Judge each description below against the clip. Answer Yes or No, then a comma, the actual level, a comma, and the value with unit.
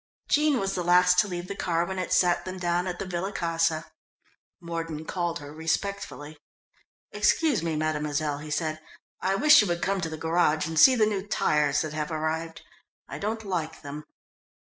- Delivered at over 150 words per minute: Yes, average, 190 wpm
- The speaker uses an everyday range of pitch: Yes, average, 3.3 semitones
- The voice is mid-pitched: Yes, medium, 170 Hz